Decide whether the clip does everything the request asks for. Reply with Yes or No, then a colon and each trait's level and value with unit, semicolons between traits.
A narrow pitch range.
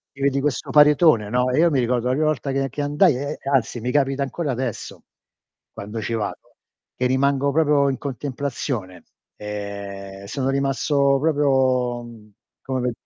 No: average, 3.2 semitones